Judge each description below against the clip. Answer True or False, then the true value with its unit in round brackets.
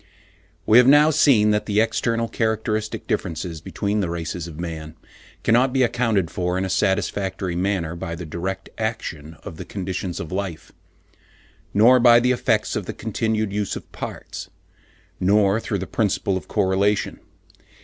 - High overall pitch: False (100 Hz)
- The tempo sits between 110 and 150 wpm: False (160 wpm)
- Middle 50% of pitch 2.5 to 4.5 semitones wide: True (4.0 semitones)